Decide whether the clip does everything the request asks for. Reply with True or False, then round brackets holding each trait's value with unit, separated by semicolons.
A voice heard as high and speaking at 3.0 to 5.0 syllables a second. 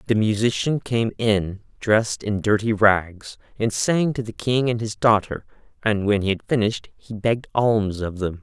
False (110 Hz; 4.6 syllables/s)